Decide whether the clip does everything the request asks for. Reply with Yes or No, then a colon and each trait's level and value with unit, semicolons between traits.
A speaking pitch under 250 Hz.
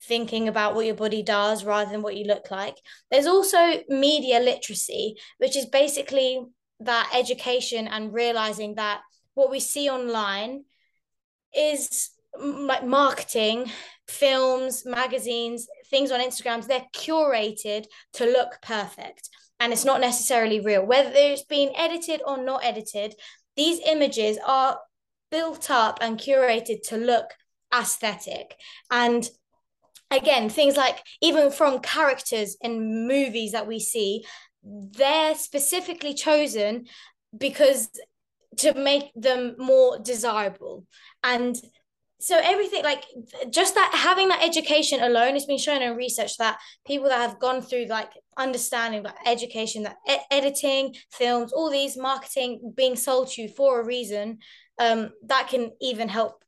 No: very high, 255 Hz